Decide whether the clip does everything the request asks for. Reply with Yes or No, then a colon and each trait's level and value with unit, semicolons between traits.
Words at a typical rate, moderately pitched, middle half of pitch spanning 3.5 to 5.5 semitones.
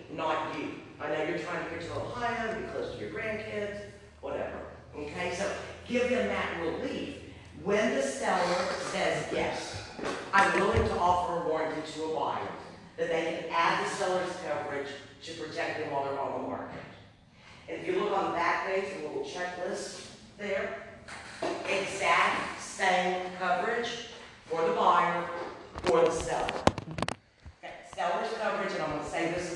Yes: average, 165 wpm; medium, 180 Hz; average, 3.9 semitones